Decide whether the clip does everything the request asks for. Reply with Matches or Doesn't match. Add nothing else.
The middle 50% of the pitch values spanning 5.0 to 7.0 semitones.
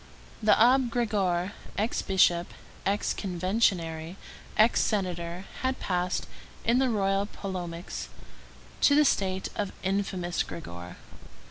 Doesn't match